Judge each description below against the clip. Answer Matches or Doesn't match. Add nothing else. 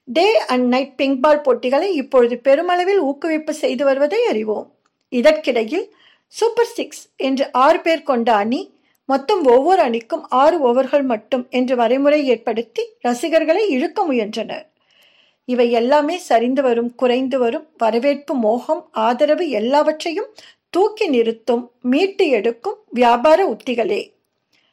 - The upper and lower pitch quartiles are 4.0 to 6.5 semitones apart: Matches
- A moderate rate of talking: Matches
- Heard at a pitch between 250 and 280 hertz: Matches